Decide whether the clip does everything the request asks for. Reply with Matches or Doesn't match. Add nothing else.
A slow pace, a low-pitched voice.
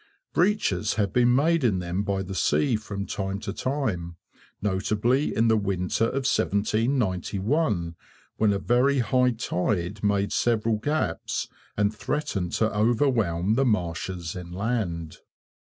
Matches